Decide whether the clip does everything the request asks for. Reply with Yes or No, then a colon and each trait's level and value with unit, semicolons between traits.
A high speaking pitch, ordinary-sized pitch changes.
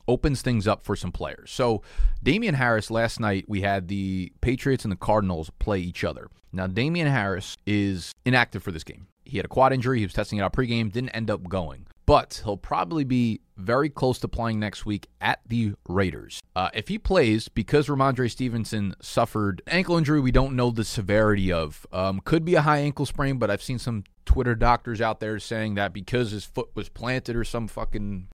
No: low, 110 Hz; average, 4.0 semitones